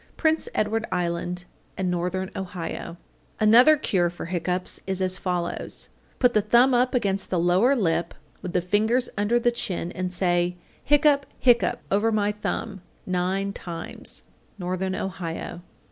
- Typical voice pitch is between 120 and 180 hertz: No, high, 190 Hz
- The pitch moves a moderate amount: Yes, average, 4.1 semitones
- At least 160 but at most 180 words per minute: No, average, 145 wpm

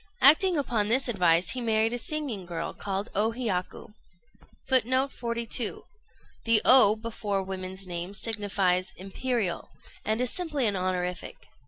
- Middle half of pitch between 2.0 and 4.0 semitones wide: No, average, 4.6 semitones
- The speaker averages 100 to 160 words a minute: Yes, slow, 135 wpm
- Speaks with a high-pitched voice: Yes, high, 215 Hz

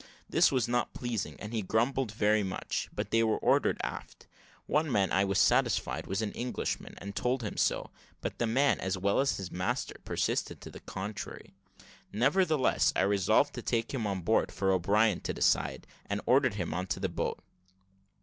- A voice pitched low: Yes, low, 105 Hz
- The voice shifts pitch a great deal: No, average, 4.0 semitones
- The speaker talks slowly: No, average, 185 wpm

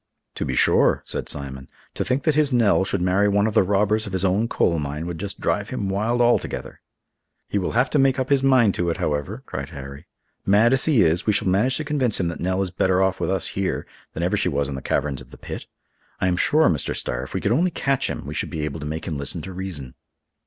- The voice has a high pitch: No, very low, 95 Hz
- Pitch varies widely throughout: Yes, wide, 6.5 semitones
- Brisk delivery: Yes, fast, 260 wpm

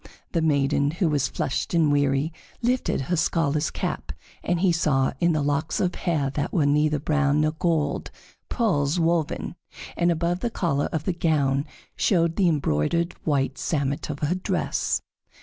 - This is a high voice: No, medium, 155 Hz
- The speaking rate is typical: Yes, average, 165 wpm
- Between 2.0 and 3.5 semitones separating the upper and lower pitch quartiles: Yes, average, 3.0 semitones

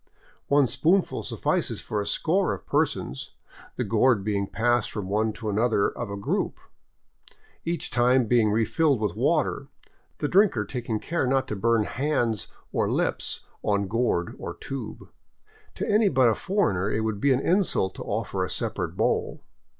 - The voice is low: Yes, low, 115 Hz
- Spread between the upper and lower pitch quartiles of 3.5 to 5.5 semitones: Yes, average, 4.8 semitones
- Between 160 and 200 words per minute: Yes, average, 165 wpm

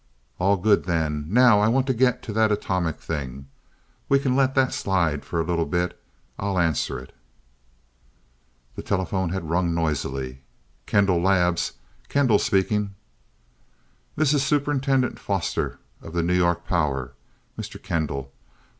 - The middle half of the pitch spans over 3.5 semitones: Yes, average, 5.2 semitones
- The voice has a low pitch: Yes, very low, 90 Hz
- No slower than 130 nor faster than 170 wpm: Yes, average, 140 wpm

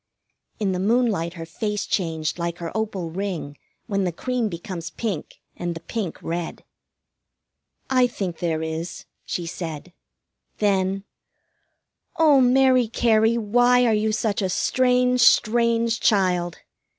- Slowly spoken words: Yes, slow, 130 wpm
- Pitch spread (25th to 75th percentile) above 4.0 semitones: Yes, average, 5.3 semitones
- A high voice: Yes, high, 200 Hz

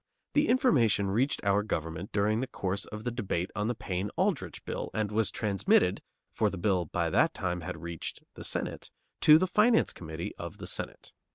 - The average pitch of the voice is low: Yes, low, 105 Hz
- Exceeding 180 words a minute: Yes, average, 190 wpm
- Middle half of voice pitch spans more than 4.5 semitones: Yes, average, 5.1 semitones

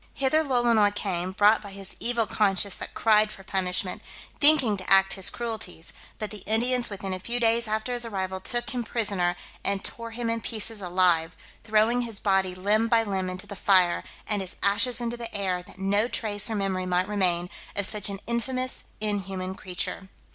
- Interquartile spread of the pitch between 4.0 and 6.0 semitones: No, average, 3.4 semitones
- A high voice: Yes, high, 205 Hz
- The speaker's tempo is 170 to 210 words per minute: Yes, average, 190 wpm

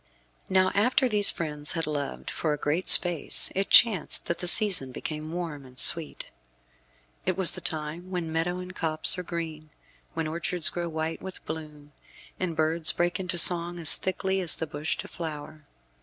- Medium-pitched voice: Yes, medium, 165 Hz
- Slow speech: No, average, 175 wpm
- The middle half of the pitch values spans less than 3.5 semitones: Yes, average, 2.7 semitones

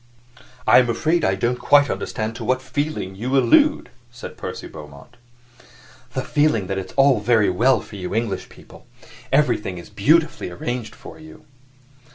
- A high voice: No, low, 120 Hz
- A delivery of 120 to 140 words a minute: No, average, 160 wpm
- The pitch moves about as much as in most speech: No, wide, 6.3 semitones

